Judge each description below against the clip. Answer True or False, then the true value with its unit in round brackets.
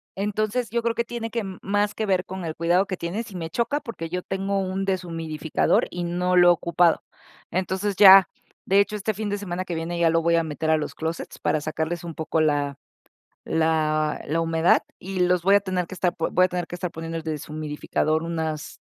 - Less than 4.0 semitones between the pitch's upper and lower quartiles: True (3.1 semitones)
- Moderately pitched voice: True (175 Hz)